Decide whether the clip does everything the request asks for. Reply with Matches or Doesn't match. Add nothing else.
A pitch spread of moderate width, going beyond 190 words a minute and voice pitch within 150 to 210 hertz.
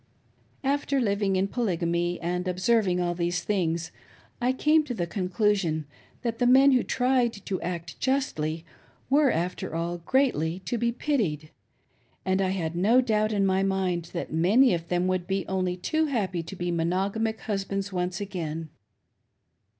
Doesn't match